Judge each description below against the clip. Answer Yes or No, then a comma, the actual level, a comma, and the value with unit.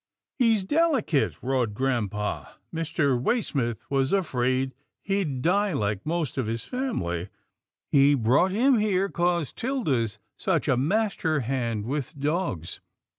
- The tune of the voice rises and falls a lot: Yes, wide, 8.0 semitones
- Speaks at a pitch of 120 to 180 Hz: Yes, medium, 140 Hz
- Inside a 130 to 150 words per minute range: Yes, slow, 135 wpm